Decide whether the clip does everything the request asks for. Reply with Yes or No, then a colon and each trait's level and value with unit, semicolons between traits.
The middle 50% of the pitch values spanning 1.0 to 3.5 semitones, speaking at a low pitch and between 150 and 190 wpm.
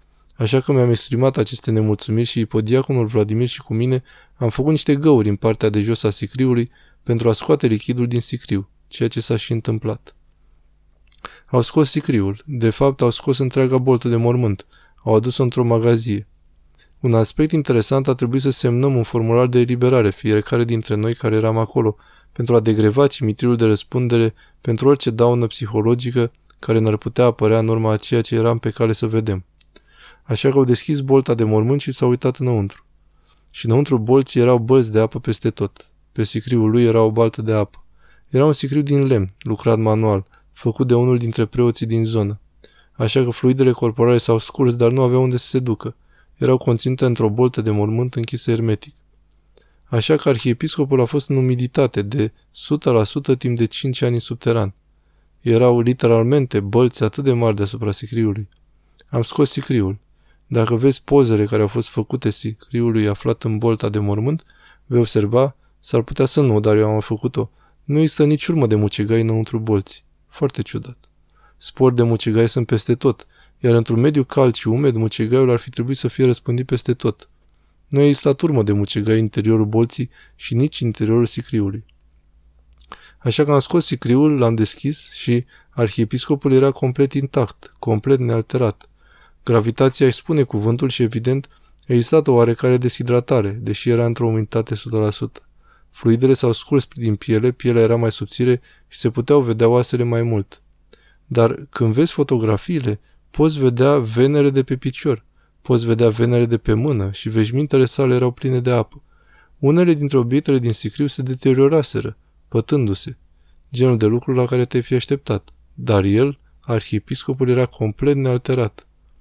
Yes: average, 3.1 semitones; low, 120 Hz; fast, 170 wpm